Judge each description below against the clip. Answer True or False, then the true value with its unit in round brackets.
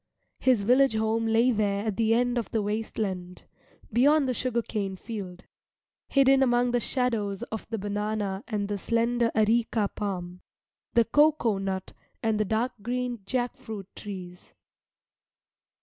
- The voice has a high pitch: True (220 Hz)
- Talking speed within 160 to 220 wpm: False (150 wpm)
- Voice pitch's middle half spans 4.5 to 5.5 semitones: False (3.2 semitones)